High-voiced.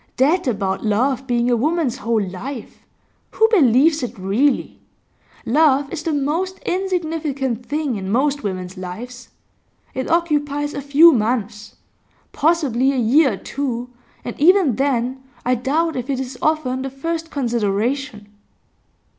Yes: very high, 265 Hz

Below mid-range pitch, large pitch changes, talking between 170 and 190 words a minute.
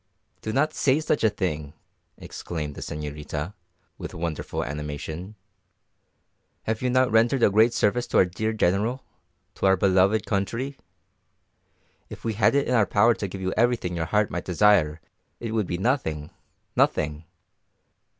No: low, 100 Hz; wide, 5.9 semitones; average, 155 wpm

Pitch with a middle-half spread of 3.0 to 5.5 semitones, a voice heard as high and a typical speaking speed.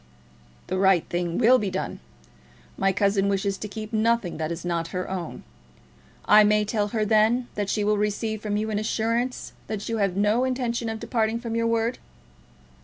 No: narrow, 2.6 semitones; high, 210 Hz; average, 190 wpm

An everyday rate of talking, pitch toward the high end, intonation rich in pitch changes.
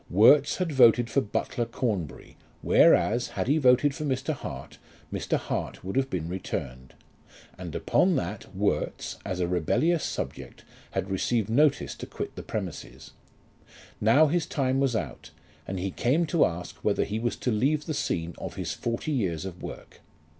No: average, 170 wpm; low, 120 Hz; wide, 7.0 semitones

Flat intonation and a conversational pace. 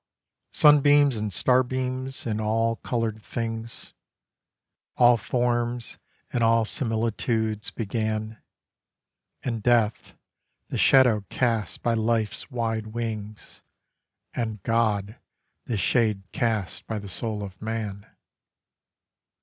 No: narrow, 1.9 semitones; slow, 100 wpm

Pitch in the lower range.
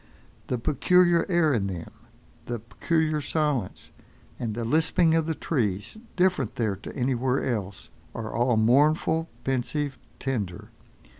Yes: low, 130 Hz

